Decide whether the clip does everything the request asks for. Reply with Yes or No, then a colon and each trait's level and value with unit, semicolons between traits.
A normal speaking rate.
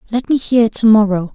No: fast, 225 wpm